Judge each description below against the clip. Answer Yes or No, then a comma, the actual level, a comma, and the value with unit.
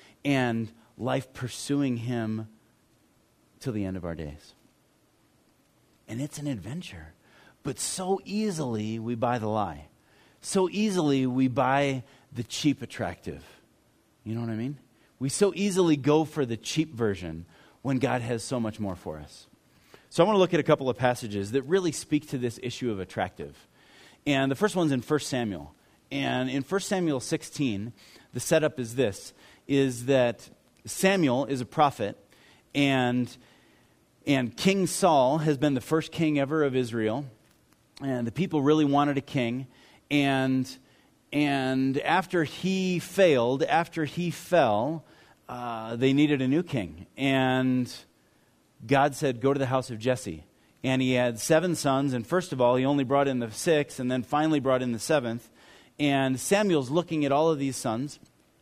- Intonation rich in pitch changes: No, average, 4.1 semitones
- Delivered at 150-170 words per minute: Yes, average, 165 wpm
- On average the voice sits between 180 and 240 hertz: No, low, 135 Hz